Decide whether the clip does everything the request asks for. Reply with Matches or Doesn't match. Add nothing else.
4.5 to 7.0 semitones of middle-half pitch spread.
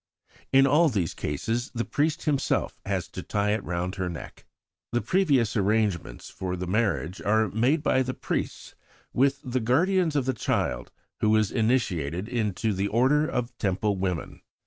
Matches